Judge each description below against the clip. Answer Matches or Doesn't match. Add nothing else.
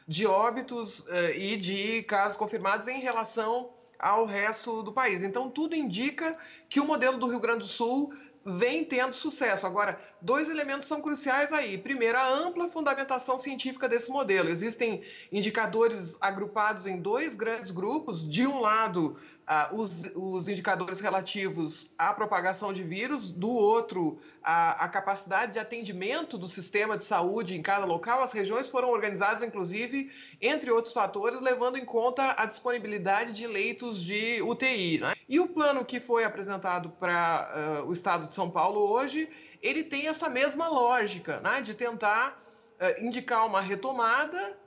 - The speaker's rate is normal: Matches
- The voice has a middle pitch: Doesn't match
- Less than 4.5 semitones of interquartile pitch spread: Doesn't match